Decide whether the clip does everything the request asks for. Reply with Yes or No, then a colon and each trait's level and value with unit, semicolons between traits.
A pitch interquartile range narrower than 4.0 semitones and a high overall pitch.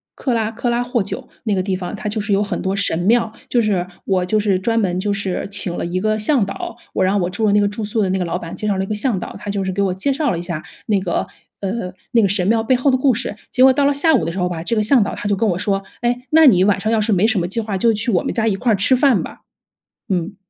Yes: average, 3.5 semitones; high, 205 Hz